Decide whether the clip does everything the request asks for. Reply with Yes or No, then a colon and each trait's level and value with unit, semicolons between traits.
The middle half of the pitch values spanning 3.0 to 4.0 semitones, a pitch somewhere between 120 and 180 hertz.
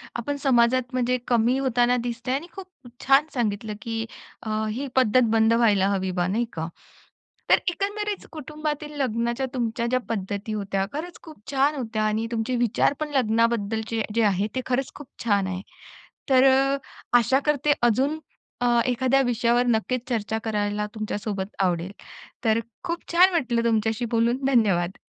No: average, 3.6 semitones; high, 235 Hz